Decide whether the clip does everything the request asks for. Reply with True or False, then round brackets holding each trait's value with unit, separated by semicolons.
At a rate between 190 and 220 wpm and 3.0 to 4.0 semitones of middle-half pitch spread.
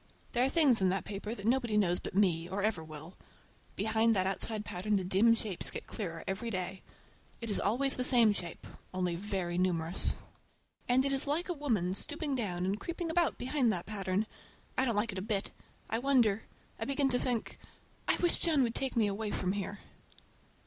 False (195 wpm; 5.0 semitones)